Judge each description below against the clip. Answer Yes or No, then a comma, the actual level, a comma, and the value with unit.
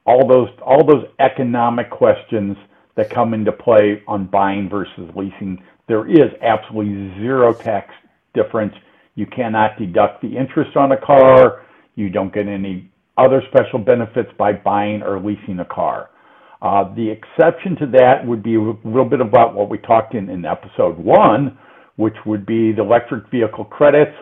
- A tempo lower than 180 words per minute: Yes, average, 165 wpm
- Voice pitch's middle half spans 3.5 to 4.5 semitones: Yes, average, 3.9 semitones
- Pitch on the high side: No, low, 110 Hz